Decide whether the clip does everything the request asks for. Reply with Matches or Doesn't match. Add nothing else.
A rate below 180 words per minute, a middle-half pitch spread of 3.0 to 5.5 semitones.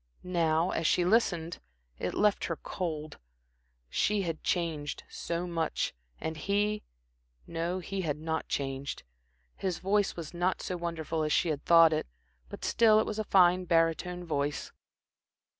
Doesn't match